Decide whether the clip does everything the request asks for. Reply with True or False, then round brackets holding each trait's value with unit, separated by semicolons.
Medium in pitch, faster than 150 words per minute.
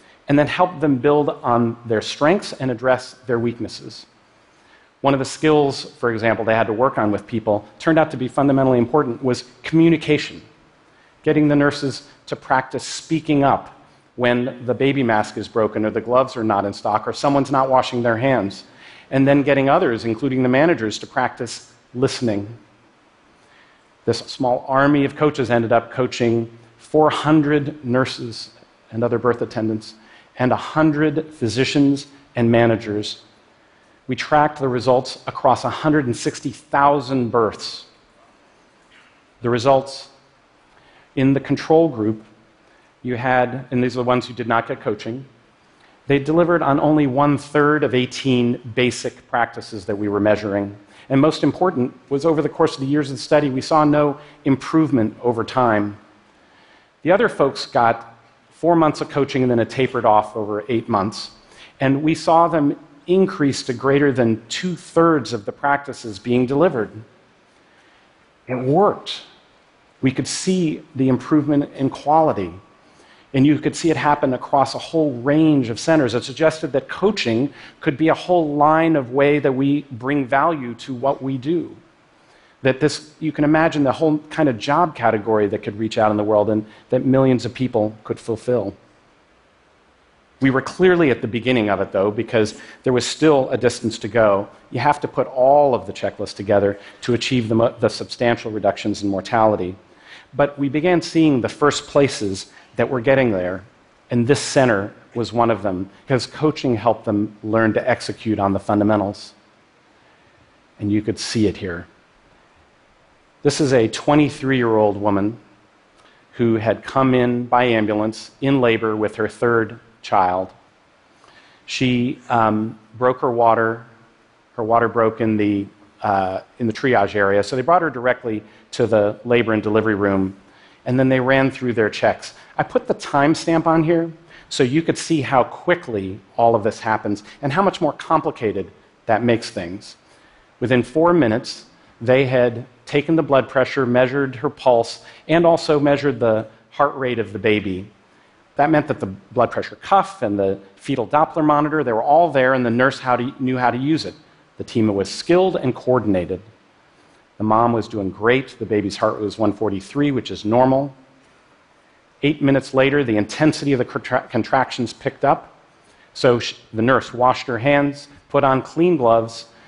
False (125 Hz; 165 wpm)